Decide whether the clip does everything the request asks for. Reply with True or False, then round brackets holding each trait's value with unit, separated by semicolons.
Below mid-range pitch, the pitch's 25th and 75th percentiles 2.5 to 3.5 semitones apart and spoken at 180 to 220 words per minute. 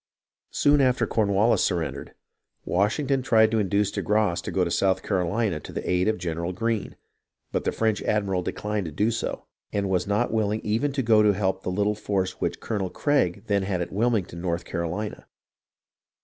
True (100 Hz; 3.2 semitones; 190 wpm)